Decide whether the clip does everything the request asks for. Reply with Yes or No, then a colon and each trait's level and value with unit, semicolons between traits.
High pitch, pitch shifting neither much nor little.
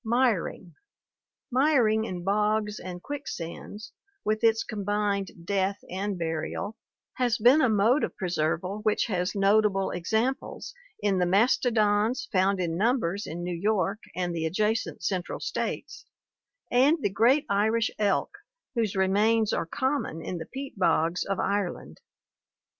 Yes: high, 205 Hz; average, 3.4 semitones